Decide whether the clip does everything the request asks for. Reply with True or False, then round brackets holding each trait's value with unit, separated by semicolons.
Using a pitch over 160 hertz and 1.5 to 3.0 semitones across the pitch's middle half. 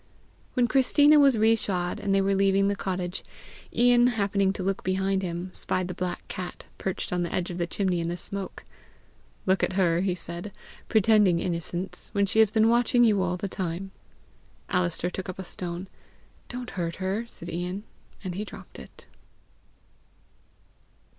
True (190 Hz; 2.7 semitones)